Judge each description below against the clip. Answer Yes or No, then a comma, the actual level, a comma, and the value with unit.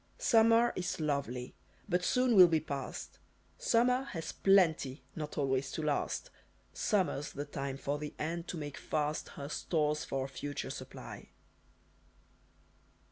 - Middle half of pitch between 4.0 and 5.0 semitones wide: Yes, average, 4.6 semitones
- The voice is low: No, medium, 155 Hz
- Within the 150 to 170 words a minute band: No, slow, 135 wpm